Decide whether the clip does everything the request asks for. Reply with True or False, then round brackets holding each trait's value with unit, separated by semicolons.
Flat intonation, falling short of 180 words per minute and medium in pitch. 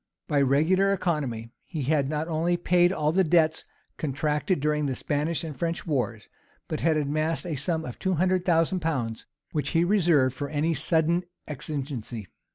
False (3.2 semitones; 165 wpm; 155 Hz)